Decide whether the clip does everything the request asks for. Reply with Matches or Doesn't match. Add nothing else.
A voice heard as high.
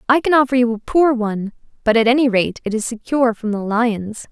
Matches